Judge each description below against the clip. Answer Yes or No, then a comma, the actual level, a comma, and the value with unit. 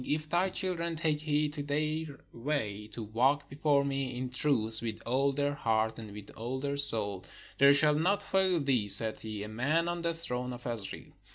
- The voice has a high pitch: No, medium, 140 Hz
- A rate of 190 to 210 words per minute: Yes, average, 195 wpm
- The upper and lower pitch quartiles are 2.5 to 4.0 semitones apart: No, average, 5.0 semitones